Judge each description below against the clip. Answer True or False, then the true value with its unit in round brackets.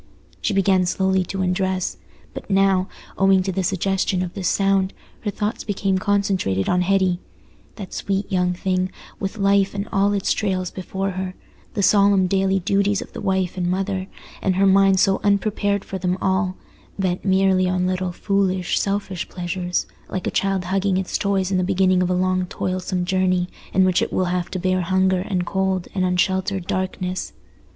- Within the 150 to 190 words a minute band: True (175 wpm)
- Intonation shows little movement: True (1.2 semitones)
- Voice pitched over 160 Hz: True (190 Hz)